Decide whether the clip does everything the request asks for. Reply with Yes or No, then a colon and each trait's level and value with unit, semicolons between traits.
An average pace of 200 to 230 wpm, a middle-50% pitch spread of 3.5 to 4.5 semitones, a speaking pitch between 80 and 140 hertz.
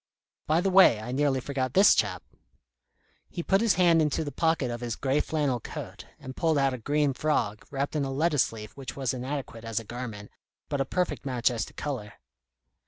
Yes: fast, 205 wpm; average, 3.9 semitones; low, 135 Hz